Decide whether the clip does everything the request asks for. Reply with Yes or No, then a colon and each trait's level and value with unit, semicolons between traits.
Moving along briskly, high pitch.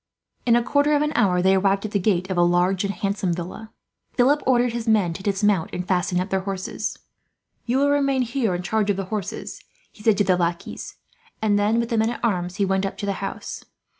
Yes: fast, 235 wpm; high, 200 Hz